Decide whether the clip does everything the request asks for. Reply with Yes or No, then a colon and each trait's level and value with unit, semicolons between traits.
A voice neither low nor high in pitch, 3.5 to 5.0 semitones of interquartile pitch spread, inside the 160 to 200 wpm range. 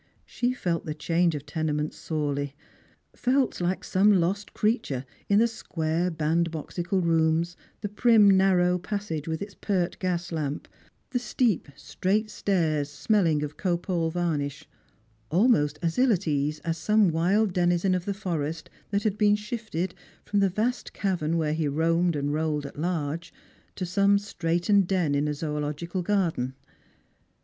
No: medium, 175 Hz; average, 4.3 semitones; average, 150 wpm